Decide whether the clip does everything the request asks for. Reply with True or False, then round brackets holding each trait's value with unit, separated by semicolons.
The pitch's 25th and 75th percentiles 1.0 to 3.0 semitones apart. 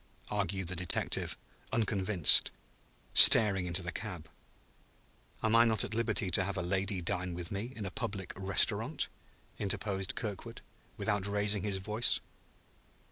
True (2.5 semitones)